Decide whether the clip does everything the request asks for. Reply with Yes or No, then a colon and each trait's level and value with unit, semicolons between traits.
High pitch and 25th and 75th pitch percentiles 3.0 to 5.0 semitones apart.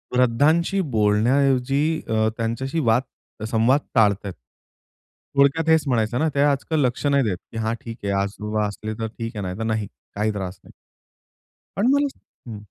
No: low, 115 Hz; average, 4.5 semitones